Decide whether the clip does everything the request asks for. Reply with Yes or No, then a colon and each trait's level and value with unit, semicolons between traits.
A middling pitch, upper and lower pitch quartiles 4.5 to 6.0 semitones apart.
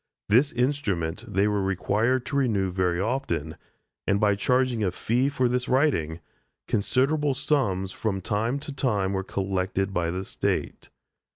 No: low, 105 Hz; average, 5.2 semitones